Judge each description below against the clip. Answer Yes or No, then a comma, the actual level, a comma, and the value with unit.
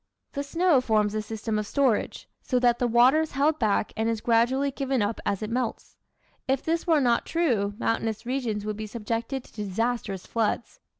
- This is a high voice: Yes, high, 235 Hz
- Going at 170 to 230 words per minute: Yes, average, 190 wpm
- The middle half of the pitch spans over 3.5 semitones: Yes, average, 3.9 semitones